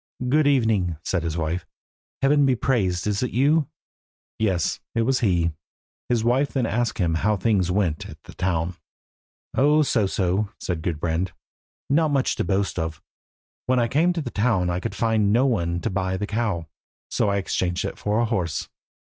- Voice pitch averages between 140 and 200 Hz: No, low, 105 Hz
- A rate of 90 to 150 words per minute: No, average, 185 wpm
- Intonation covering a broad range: Yes, wide, 5.8 semitones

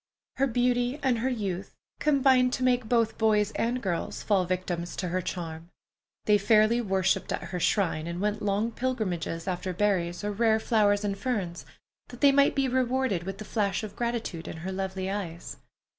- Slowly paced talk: No, average, 180 wpm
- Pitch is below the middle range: No, high, 210 Hz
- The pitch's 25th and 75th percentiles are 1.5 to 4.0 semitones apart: No, average, 4.7 semitones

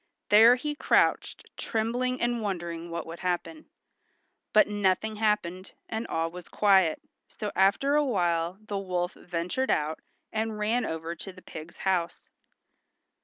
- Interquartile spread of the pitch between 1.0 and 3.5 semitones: No, average, 4.4 semitones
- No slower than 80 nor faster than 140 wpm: Yes, slow, 135 wpm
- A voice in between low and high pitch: No, high, 195 Hz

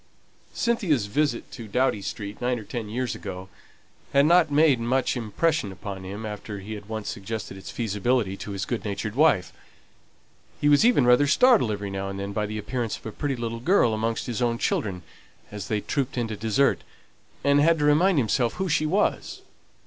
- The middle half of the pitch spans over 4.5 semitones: Yes, wide, 5.5 semitones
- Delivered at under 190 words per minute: No, average, 195 wpm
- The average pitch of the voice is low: Yes, low, 115 Hz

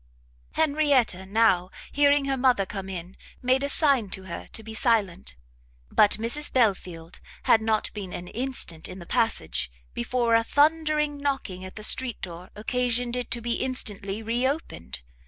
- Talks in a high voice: Yes, high, 230 Hz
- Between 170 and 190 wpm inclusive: No, average, 160 wpm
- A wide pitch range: Yes, wide, 5.7 semitones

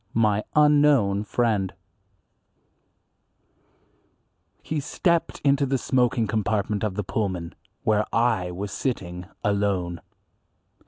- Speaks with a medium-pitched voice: No, low, 105 Hz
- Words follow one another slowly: Yes, slow, 100 wpm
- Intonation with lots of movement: No, average, 4.5 semitones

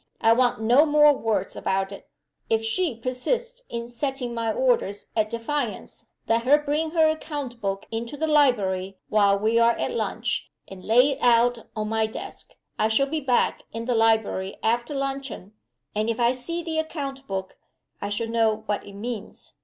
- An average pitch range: Yes, average, 4.4 semitones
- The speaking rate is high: No, average, 175 wpm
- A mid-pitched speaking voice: No, high, 235 Hz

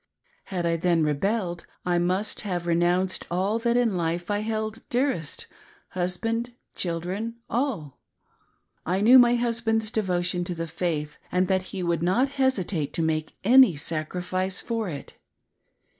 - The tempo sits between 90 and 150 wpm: Yes, average, 145 wpm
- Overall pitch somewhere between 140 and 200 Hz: Yes, medium, 185 Hz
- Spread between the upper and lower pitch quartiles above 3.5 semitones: Yes, average, 4.6 semitones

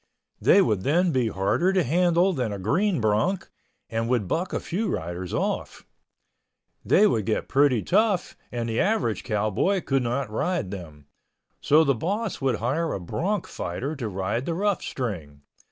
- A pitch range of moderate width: No, wide, 8.9 semitones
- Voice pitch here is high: No, low, 130 Hz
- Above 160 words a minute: Yes, average, 170 wpm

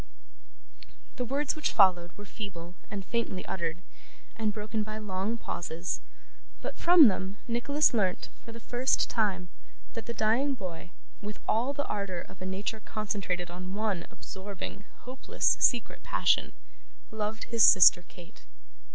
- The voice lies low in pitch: No, high, 210 Hz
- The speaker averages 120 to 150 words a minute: Yes, average, 145 wpm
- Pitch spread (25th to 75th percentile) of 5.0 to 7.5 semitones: No, average, 4.0 semitones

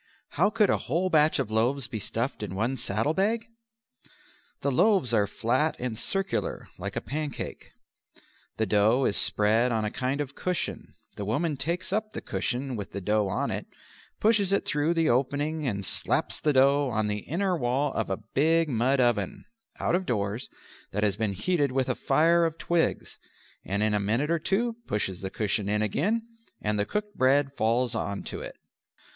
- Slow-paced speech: No, average, 185 wpm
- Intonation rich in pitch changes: Yes, wide, 7.1 semitones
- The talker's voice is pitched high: No, low, 130 Hz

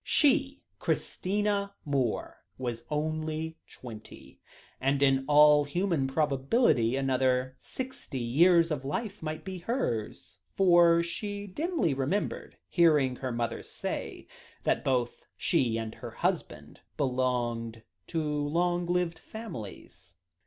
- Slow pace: Yes, slow, 110 wpm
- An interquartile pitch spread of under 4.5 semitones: No, wide, 5.6 semitones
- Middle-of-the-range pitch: Yes, medium, 150 Hz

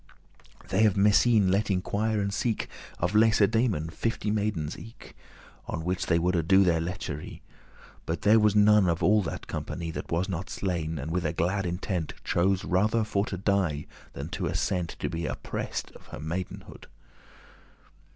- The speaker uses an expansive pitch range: No, average, 3.8 semitones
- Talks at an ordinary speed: Yes, average, 165 wpm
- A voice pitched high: No, very low, 95 Hz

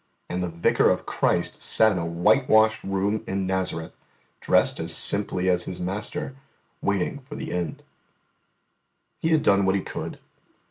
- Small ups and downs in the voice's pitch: No, average, 3.4 semitones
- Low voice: Yes, very low, 95 Hz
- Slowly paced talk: No, average, 155 wpm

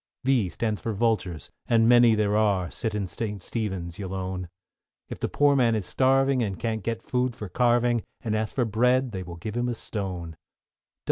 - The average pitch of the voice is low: Yes, low, 110 Hz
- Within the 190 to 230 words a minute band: Yes, average, 195 wpm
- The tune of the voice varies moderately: Yes, average, 4.0 semitones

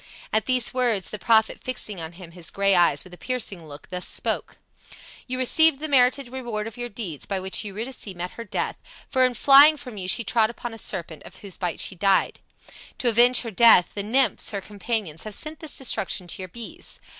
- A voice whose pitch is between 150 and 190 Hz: No, high, 220 Hz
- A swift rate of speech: Yes, fast, 215 wpm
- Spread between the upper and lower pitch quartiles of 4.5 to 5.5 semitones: Yes, average, 5.1 semitones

